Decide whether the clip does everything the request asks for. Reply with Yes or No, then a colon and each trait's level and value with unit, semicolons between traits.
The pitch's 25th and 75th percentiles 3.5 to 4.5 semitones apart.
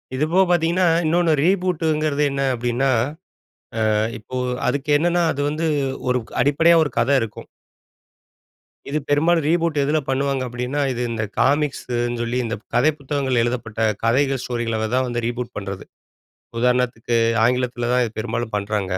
Yes: average, 4.2 semitones